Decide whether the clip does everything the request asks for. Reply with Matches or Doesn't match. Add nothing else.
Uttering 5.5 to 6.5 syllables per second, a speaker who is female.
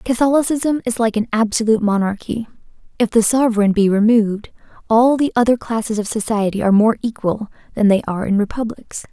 Matches